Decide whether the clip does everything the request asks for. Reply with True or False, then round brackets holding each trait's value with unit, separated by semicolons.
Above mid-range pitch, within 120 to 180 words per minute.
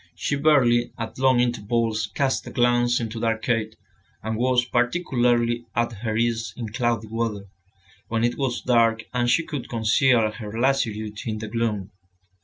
False (120 Hz; 160 wpm)